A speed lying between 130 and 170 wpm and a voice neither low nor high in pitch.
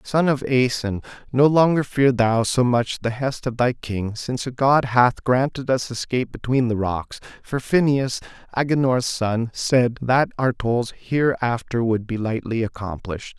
No: average, 165 wpm; low, 125 Hz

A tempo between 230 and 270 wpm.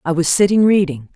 No: fast, 205 wpm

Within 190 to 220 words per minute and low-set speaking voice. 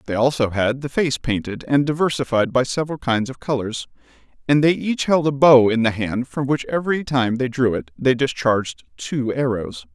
Yes: average, 200 wpm; low, 130 Hz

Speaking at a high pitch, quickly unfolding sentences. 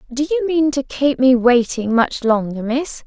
No: very high, 265 Hz; average, 195 wpm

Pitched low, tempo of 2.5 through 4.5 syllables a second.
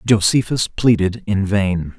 Yes: low, 100 Hz; 3.9 syllables/s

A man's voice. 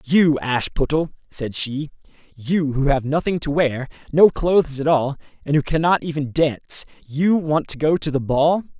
Yes: male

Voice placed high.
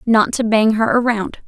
Yes: high, 225 Hz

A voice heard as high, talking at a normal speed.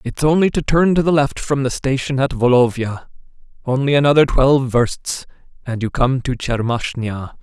No: low, 135 Hz; average, 170 wpm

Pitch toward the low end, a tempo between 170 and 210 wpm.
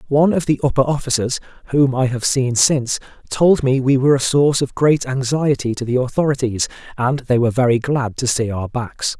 Yes: low, 130 Hz; average, 200 wpm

